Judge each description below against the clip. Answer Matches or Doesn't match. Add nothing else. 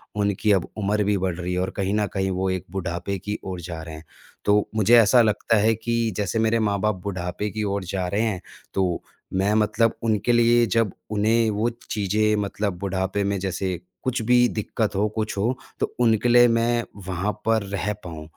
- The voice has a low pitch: Matches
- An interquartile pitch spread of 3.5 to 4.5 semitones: Doesn't match